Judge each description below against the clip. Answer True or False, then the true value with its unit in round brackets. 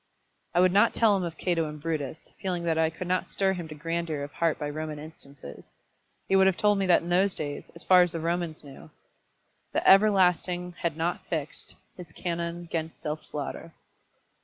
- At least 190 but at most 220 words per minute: True (200 wpm)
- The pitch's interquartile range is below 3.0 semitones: True (2.5 semitones)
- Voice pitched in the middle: True (170 Hz)